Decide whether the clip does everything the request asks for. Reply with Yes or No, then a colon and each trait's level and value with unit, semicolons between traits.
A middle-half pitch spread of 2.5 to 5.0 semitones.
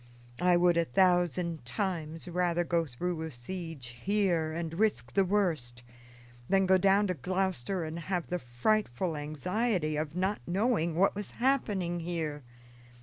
Yes: average, 3.3 semitones